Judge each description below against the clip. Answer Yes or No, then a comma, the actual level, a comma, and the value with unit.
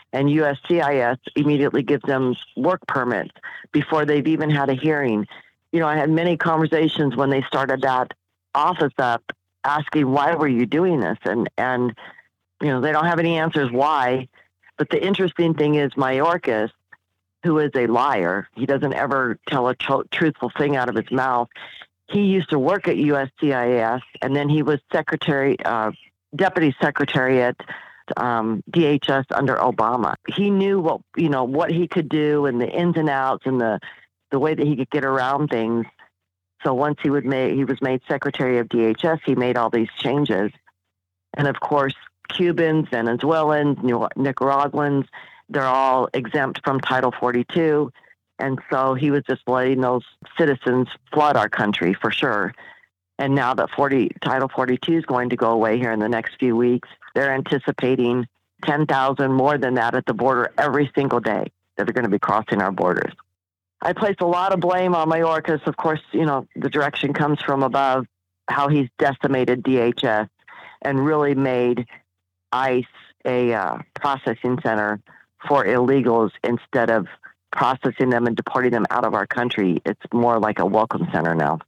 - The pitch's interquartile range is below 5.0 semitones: Yes, average, 3.5 semitones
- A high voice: No, low, 135 Hz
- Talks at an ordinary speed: Yes, average, 170 wpm